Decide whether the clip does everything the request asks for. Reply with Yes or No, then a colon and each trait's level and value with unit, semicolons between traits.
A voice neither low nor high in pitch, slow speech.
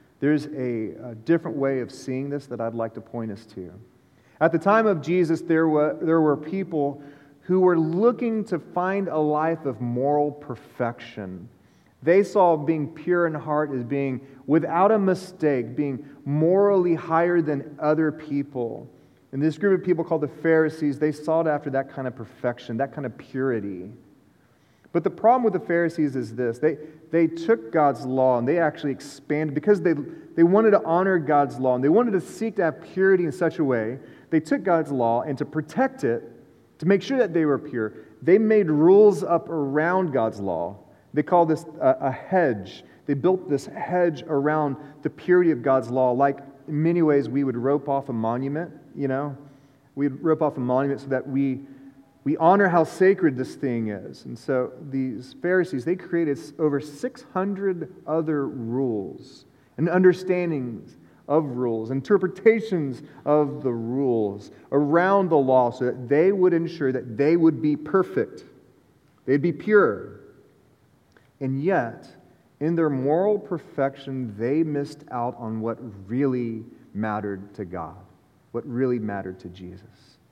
No: medium, 150 Hz; average, 170 wpm